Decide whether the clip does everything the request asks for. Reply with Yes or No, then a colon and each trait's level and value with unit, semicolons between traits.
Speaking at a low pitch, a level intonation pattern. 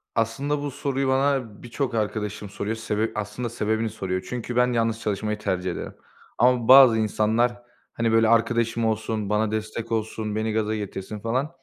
Yes: low, 110 Hz; narrow, 2.2 semitones